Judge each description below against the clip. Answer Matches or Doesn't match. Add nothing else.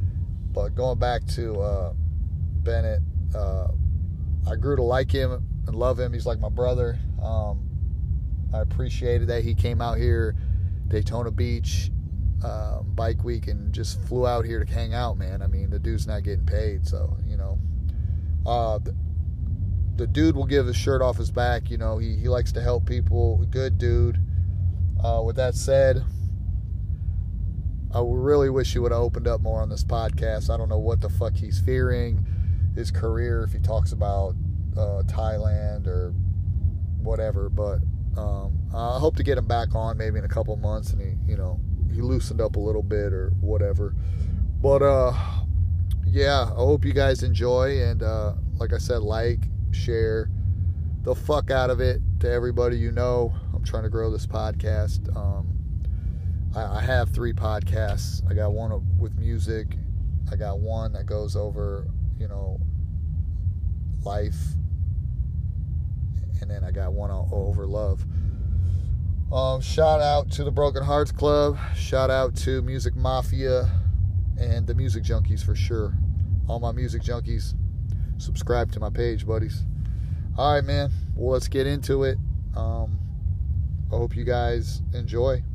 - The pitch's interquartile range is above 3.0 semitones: Doesn't match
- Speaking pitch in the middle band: Doesn't match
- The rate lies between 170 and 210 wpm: Doesn't match